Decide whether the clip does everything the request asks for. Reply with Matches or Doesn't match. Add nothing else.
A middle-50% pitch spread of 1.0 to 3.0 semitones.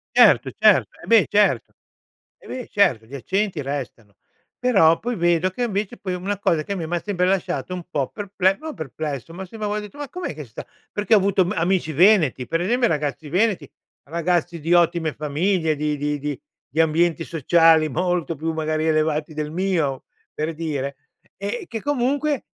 Doesn't match